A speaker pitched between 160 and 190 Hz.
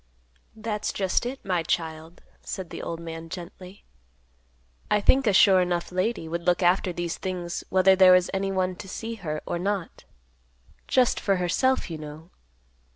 Yes: medium, 185 Hz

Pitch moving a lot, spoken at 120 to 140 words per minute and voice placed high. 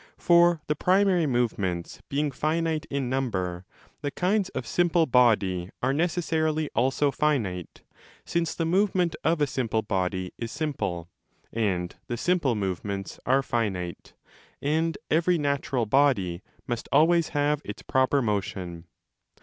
No: wide, 7.7 semitones; slow, 135 wpm; low, 135 Hz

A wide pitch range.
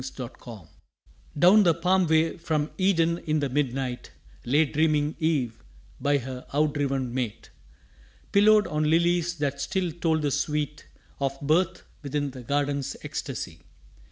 No: average, 3.3 semitones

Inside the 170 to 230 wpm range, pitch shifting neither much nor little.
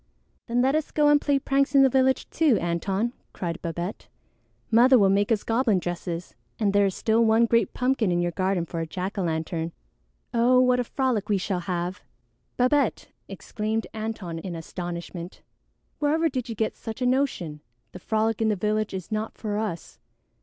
No: average, 185 wpm; wide, 5.7 semitones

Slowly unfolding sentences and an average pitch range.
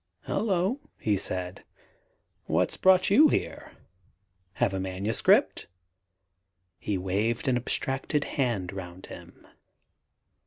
No: slow, 95 wpm; wide, 7.7 semitones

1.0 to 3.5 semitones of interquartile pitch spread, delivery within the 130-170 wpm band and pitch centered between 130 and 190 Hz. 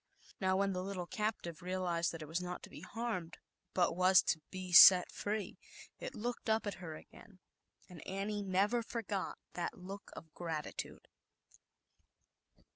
Yes: average, 2.7 semitones; average, 160 wpm; medium, 185 Hz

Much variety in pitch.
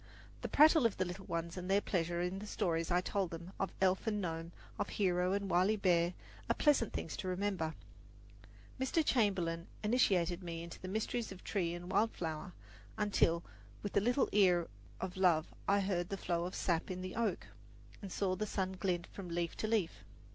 No: average, 2.8 semitones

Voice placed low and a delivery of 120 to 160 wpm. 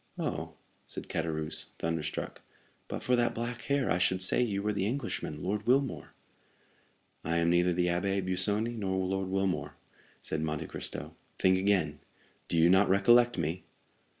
Yes: very low, 95 Hz; average, 150 wpm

